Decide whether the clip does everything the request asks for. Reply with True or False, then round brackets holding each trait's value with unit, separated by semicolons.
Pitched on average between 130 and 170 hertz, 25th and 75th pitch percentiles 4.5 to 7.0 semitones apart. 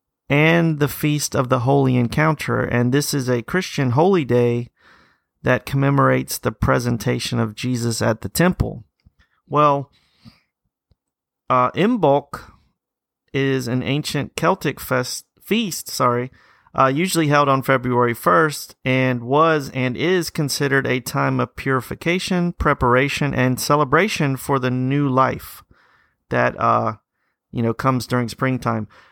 False (135 Hz; 3.2 semitones)